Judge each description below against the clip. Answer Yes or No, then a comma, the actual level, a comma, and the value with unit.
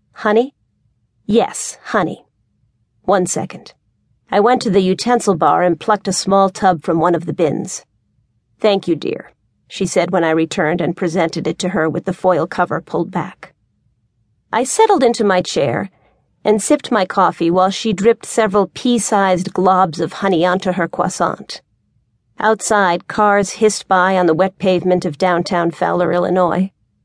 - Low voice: No, medium, 180 Hz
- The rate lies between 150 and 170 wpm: Yes, average, 160 wpm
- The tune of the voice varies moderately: Yes, average, 3.3 semitones